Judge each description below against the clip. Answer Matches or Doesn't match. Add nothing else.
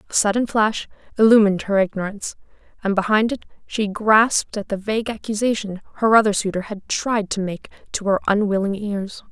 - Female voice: Matches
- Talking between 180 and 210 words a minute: Doesn't match